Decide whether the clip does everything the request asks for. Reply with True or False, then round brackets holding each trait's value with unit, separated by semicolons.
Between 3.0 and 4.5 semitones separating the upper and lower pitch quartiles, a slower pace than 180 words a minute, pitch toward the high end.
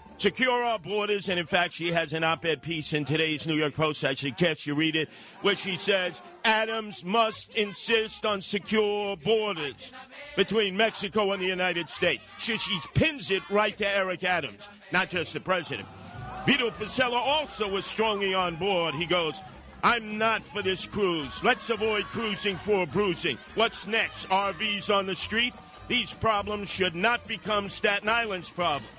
True (3.6 semitones; 170 wpm; 200 Hz)